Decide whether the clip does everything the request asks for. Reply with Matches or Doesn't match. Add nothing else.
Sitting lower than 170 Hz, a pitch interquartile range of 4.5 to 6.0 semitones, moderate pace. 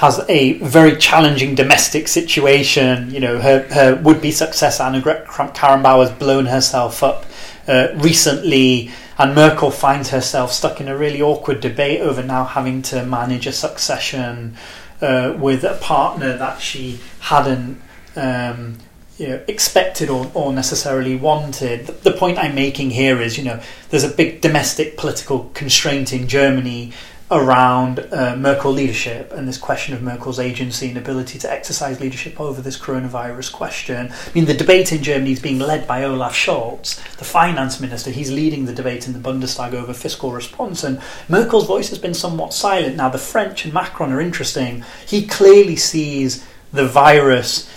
Doesn't match